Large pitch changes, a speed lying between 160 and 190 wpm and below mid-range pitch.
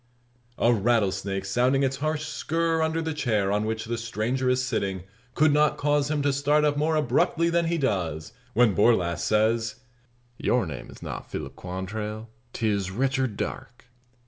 Yes: wide, 6.1 semitones; average, 165 wpm; low, 120 Hz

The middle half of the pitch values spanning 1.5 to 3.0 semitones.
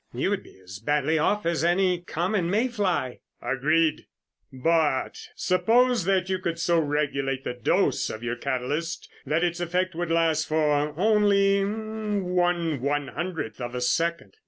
No: average, 4.2 semitones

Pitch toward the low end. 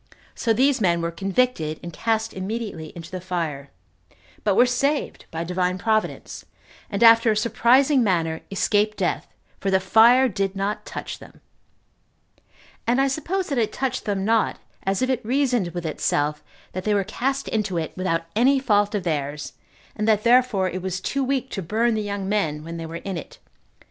No: high, 205 Hz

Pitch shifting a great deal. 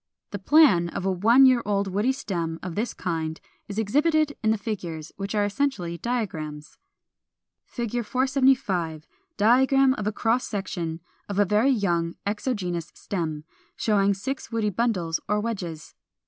Yes: wide, 5.7 semitones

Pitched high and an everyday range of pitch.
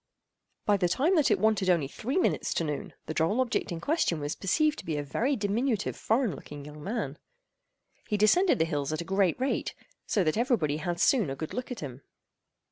No: high, 195 Hz; wide, 7.8 semitones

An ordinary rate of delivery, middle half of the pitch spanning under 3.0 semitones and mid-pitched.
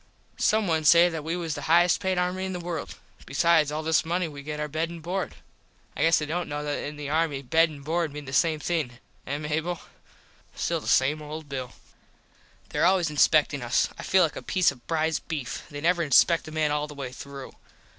No: fast, 225 wpm; narrow, 2.5 semitones; medium, 155 Hz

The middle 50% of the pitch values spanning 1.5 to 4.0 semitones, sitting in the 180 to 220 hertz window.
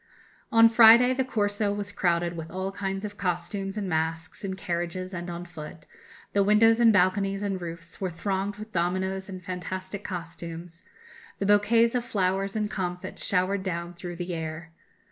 Yes: average, 2.8 semitones; high, 190 Hz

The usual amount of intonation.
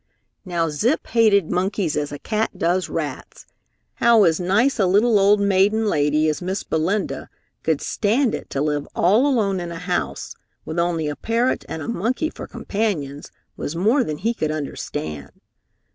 No: wide, 5.8 semitones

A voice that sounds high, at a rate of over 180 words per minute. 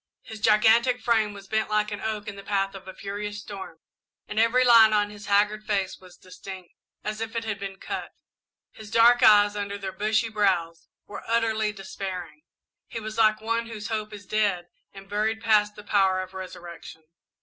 Yes: high, 210 Hz; average, 190 wpm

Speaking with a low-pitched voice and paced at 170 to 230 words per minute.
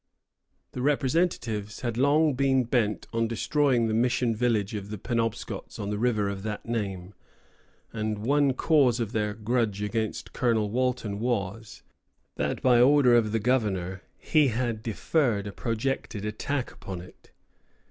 No: low, 115 Hz; average, 145 wpm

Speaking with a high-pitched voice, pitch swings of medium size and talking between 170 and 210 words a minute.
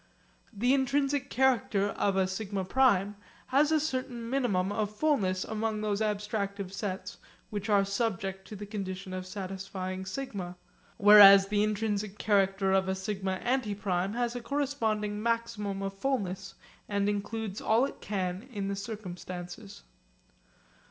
No: high, 205 Hz; average, 3.0 semitones; average, 140 wpm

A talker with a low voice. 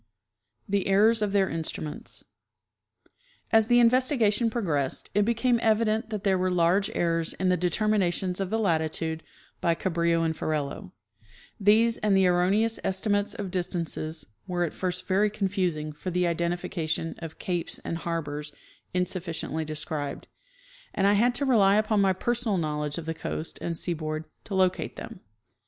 No: medium, 185 Hz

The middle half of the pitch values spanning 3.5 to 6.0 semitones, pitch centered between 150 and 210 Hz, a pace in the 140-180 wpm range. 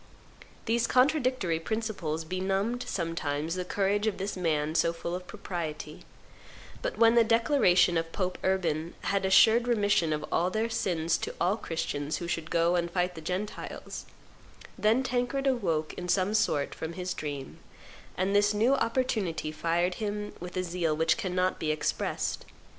Yes: average, 4.5 semitones; medium, 185 Hz; average, 160 wpm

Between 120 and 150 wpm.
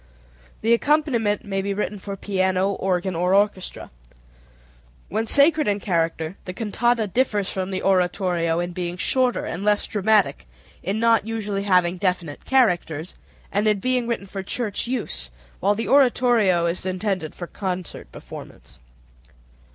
Yes: average, 145 wpm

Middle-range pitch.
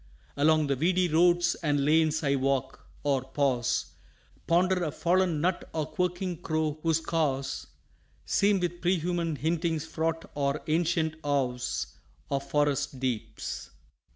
Yes: medium, 155 Hz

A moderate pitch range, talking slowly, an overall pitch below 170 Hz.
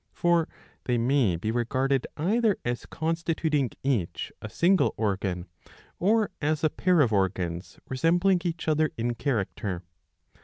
No: wide, 7.2 semitones; slow, 130 wpm; low, 135 Hz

